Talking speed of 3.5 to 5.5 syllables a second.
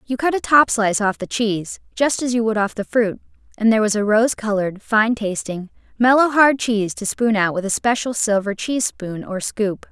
Yes: 5.3 syllables/s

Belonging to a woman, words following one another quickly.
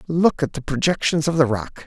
No: male; fast, 225 wpm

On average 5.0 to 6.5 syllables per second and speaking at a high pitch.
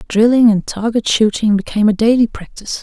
Yes: 6.0 syllables/s; high, 220 Hz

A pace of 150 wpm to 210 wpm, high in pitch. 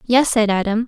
Yes: fast, 205 wpm; high, 225 Hz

